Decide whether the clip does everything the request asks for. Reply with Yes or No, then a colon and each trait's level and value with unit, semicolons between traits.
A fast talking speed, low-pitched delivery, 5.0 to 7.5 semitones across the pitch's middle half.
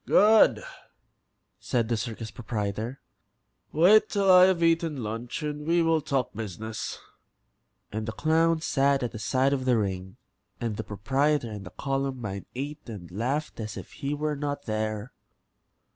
No: average, 155 wpm; low, 130 Hz; wide, 5.6 semitones